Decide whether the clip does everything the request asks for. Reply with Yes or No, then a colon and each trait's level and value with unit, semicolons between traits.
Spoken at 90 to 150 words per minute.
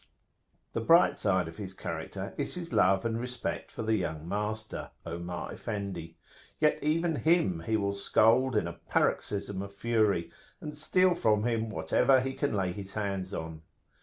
No: average, 165 wpm